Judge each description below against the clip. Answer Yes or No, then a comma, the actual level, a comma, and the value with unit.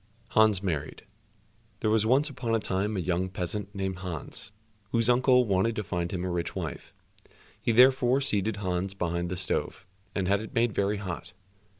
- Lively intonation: No, average, 3.8 semitones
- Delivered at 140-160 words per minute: No, average, 185 wpm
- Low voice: Yes, low, 100 Hz